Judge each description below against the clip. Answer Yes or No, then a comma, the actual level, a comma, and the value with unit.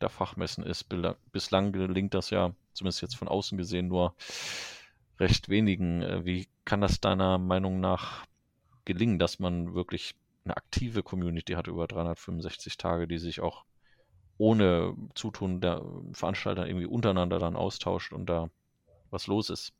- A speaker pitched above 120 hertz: No, very low, 90 Hz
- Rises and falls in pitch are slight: Yes, narrow, 2.0 semitones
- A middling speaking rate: Yes, average, 145 wpm